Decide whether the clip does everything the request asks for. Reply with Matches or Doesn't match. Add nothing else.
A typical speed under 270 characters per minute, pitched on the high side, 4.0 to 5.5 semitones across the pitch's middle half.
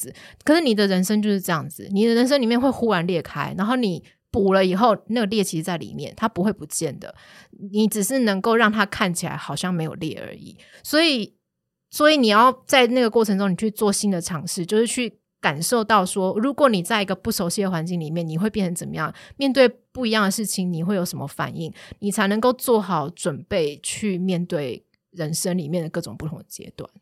Doesn't match